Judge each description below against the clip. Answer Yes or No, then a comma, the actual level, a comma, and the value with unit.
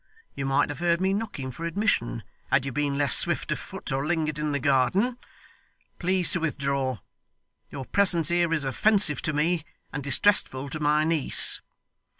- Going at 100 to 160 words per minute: No, average, 170 wpm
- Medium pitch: Yes, medium, 150 Hz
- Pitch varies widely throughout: No, average, 4.0 semitones